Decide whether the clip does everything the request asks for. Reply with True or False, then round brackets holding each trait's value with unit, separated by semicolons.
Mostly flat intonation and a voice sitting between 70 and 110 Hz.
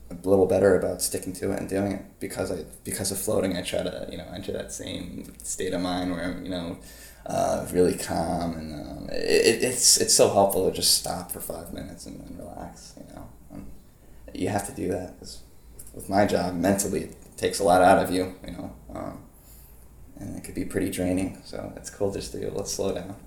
True (2.1 semitones; 90 Hz)